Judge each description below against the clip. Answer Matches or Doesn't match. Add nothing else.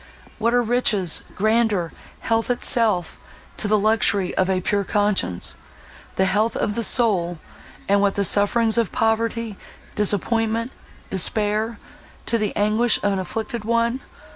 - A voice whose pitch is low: Doesn't match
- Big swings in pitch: Doesn't match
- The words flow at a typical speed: Doesn't match